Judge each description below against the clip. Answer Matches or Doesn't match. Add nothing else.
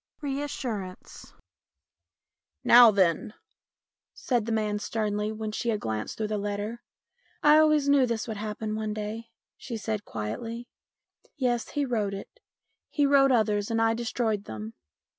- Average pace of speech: Matches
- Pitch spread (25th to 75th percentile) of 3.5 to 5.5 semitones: Doesn't match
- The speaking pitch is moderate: Doesn't match